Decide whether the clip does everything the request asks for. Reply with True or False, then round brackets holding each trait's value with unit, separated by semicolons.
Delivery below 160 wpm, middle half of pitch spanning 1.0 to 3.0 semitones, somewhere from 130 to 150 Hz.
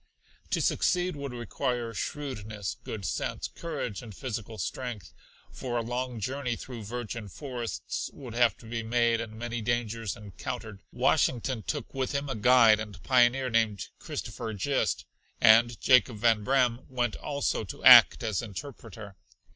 False (145 wpm; 2.7 semitones; 120 Hz)